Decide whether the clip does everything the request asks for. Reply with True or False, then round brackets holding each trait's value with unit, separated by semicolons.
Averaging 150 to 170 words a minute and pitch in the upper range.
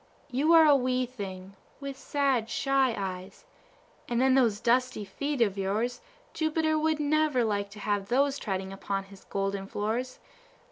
True (155 wpm; 245 Hz)